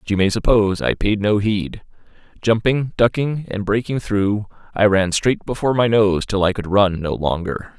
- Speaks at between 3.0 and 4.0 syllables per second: No, 4.9 syllables/s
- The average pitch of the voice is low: Yes, low, 105 Hz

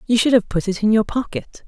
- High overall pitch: Yes, high, 220 Hz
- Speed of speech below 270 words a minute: No, fast, 285 wpm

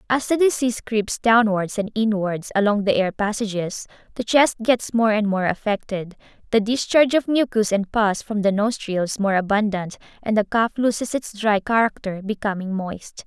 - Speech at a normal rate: Yes, average, 170 wpm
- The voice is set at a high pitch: Yes, high, 215 Hz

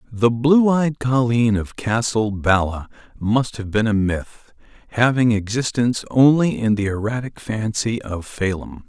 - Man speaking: Yes, male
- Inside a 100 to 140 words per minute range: Yes, slow, 135 wpm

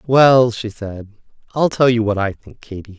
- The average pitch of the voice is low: Yes, low, 115 Hz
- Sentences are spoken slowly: No, average, 200 wpm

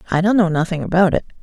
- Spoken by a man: No, female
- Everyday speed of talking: No, fast, 255 wpm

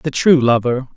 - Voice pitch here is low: Yes, low, 130 Hz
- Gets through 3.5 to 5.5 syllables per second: Yes, 4.6 syllables/s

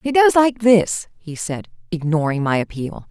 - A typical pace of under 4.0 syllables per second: No, 4.4 syllables/s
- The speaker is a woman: Yes, female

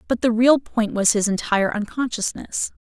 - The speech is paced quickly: No, average, 170 wpm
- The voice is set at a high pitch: Yes, high, 225 Hz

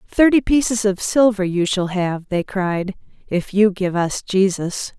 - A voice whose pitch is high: Yes, high, 200 Hz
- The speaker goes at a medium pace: Yes, average, 170 wpm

